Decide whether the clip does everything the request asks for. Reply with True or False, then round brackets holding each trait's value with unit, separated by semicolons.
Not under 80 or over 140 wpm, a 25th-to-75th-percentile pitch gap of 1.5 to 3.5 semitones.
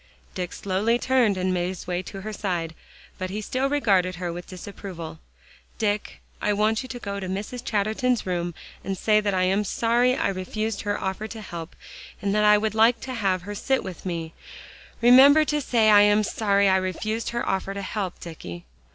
False (195 wpm; 3.1 semitones)